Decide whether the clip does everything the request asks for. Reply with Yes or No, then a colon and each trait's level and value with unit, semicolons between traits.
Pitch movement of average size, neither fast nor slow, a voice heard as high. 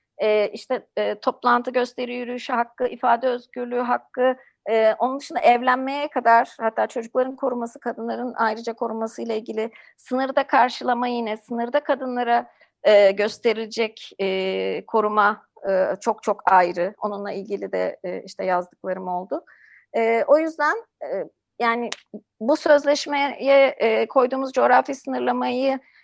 Yes: average, 3.4 semitones; average, 125 wpm; high, 235 Hz